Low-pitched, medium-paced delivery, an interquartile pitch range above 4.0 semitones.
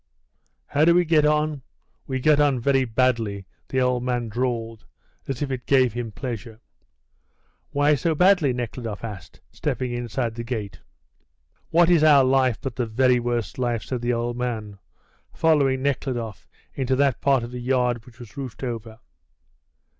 No: low, 125 Hz; average, 160 wpm; average, 2.7 semitones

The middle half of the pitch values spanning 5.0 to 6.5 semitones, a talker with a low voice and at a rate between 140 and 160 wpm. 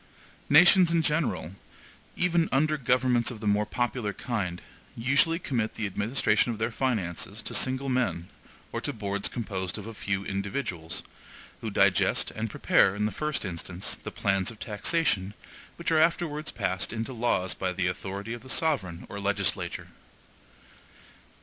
Yes: wide, 5.6 semitones; low, 110 Hz; average, 155 wpm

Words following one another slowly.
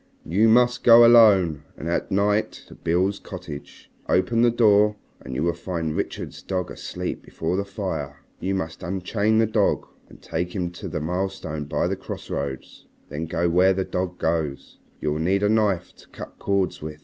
No: average, 185 wpm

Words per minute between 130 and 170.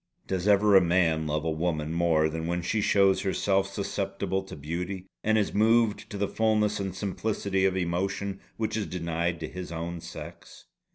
No: average, 180 wpm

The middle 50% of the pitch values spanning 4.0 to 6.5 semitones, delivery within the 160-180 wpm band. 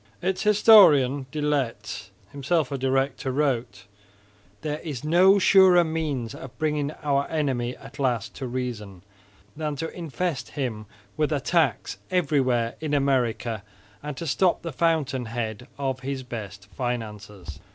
No: average, 4.3 semitones; slow, 135 wpm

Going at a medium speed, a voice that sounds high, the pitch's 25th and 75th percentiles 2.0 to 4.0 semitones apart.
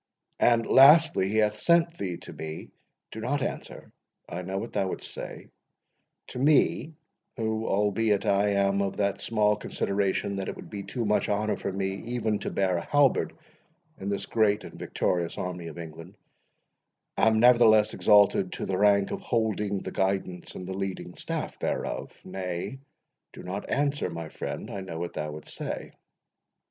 No: average, 160 wpm; low, 100 Hz; average, 2.9 semitones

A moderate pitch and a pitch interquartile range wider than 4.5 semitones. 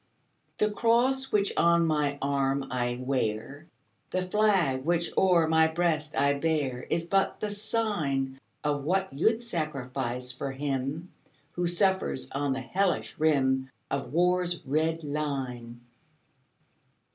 Yes: medium, 155 Hz; average, 4.9 semitones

